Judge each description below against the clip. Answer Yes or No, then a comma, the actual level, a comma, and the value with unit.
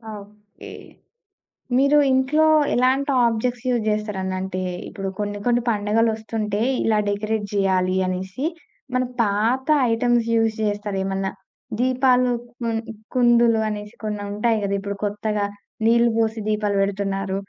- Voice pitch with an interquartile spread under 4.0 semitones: Yes, average, 2.7 semitones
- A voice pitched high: Yes, high, 215 Hz